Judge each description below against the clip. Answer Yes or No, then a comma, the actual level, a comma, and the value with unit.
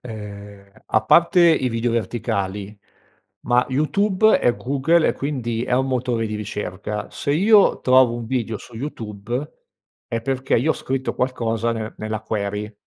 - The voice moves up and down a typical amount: Yes, average, 3.7 semitones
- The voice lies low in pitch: Yes, low, 120 Hz